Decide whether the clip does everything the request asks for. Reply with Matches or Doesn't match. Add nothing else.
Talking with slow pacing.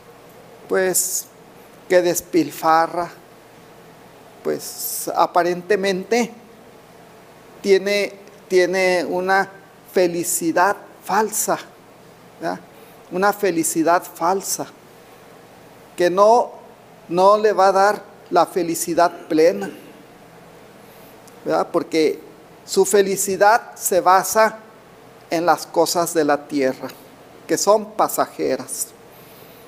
Matches